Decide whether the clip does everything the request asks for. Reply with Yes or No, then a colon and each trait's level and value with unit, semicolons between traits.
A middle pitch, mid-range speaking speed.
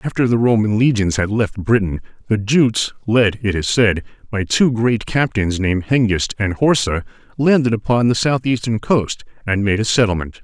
No: low, 110 Hz; average, 170 wpm